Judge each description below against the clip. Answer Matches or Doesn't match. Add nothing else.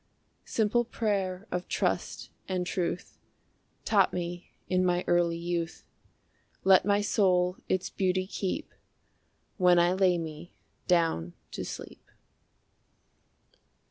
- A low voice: Doesn't match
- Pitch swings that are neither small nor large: Doesn't match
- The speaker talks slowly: Matches